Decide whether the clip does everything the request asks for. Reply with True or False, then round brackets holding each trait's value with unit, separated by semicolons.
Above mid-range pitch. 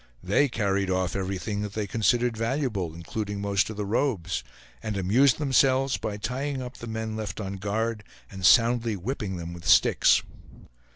False (105 Hz)